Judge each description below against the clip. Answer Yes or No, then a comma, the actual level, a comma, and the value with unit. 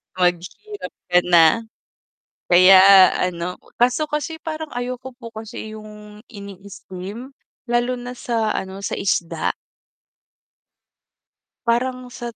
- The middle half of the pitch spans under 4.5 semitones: No, average, 4.8 semitones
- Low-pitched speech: No, high, 220 Hz